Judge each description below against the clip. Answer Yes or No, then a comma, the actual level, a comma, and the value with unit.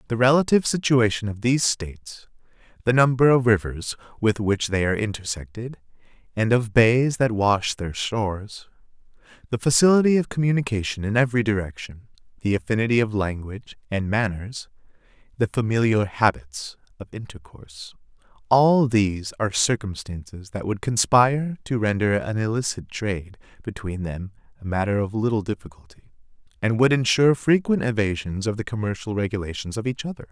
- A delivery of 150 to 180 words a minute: No, average, 140 wpm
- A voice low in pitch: Yes, low, 110 Hz